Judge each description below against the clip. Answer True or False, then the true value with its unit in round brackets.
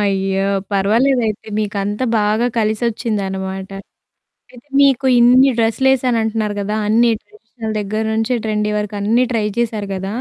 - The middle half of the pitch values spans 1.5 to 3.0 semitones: True (2.7 semitones)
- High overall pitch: True (215 Hz)